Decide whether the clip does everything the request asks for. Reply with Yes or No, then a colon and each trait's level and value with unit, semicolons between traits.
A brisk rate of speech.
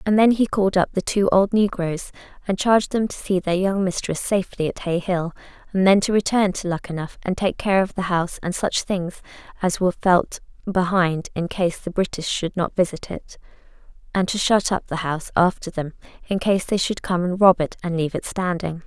Yes: fast, 215 wpm